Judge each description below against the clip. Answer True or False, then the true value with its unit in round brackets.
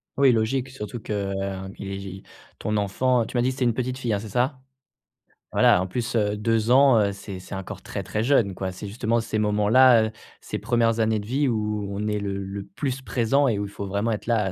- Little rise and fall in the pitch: False (3.3 semitones)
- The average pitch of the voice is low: True (110 Hz)